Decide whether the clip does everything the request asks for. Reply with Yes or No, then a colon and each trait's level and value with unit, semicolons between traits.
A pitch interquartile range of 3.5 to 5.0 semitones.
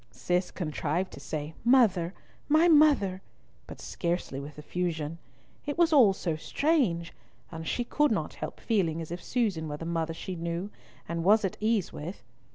No: wide, 5.4 semitones